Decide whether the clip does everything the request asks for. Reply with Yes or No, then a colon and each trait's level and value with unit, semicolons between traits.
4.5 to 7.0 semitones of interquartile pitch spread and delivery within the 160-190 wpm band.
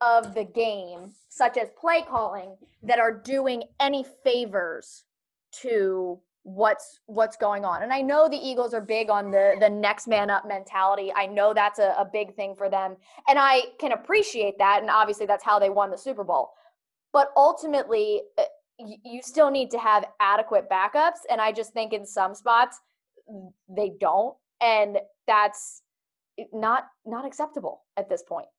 Yes: wide, 5.4 semitones; average, 170 wpm